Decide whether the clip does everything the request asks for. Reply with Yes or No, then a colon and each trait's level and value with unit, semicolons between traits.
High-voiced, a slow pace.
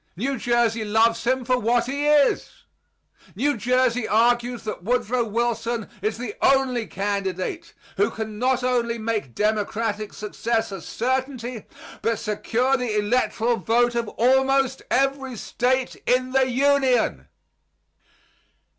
Yes: high, 240 Hz; slow, 125 wpm